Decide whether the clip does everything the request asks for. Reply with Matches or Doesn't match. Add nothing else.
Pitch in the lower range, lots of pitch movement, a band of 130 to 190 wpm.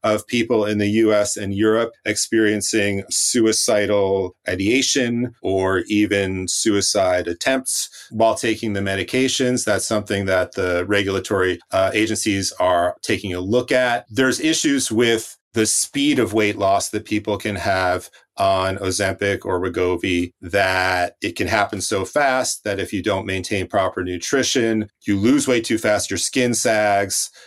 Doesn't match